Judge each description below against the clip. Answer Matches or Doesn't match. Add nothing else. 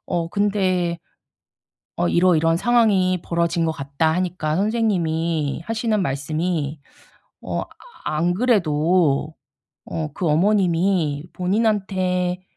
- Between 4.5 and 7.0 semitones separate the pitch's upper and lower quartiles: Doesn't match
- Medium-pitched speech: Matches